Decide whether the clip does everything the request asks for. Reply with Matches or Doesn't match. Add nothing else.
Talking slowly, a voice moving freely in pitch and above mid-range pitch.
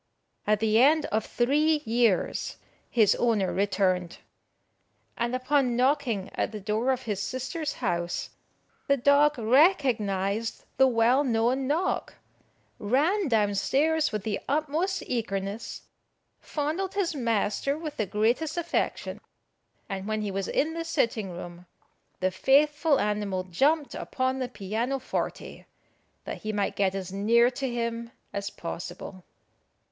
Matches